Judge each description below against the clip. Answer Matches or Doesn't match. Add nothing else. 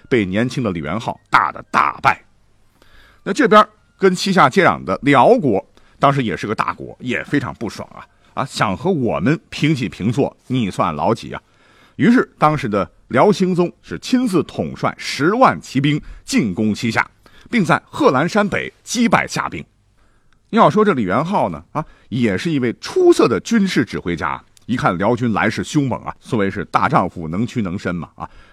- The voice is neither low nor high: Matches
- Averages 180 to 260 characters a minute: Matches